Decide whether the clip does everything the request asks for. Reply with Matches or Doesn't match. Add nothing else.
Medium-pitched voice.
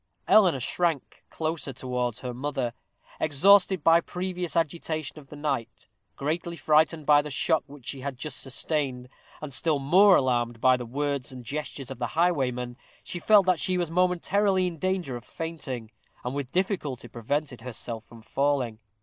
Matches